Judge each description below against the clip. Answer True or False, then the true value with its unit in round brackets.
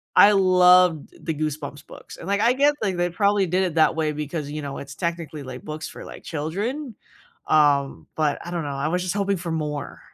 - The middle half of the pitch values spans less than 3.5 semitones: False (3.8 semitones)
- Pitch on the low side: False (165 Hz)